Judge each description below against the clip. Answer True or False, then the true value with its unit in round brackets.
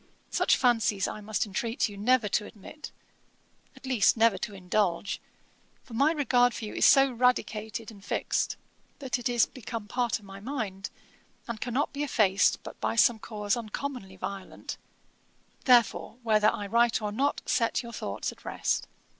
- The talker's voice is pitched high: True (225 Hz)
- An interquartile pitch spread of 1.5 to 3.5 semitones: True (3.2 semitones)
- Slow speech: False (165 wpm)